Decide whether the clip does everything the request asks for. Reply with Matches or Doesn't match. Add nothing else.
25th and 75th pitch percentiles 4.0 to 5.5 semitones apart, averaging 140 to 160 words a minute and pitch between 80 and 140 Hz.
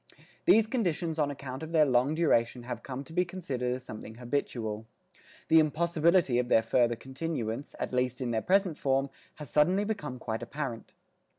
Doesn't match